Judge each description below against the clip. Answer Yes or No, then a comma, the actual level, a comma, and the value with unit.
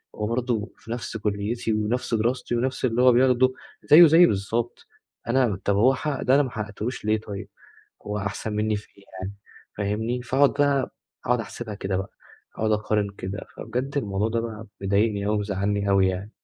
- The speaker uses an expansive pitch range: No, average, 3.3 semitones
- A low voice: Yes, low, 110 Hz